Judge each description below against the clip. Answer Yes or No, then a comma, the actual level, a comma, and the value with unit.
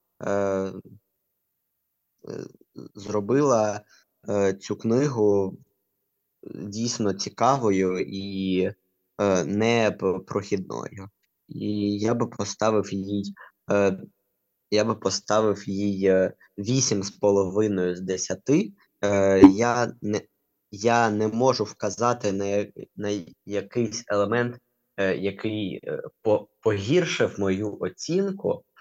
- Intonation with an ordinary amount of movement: No, narrow, 2.1 semitones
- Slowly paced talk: Yes, slow, 70 wpm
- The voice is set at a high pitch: No, low, 100 Hz